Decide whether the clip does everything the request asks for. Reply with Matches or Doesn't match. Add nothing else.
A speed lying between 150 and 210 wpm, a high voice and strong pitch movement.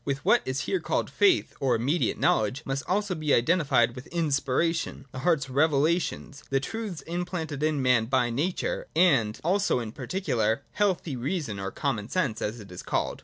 Doesn't match